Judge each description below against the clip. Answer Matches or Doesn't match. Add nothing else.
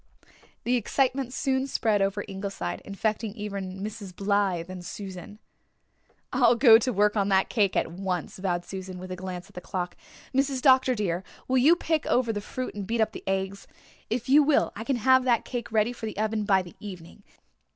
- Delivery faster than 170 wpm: Matches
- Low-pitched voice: Doesn't match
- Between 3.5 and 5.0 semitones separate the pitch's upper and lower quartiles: Matches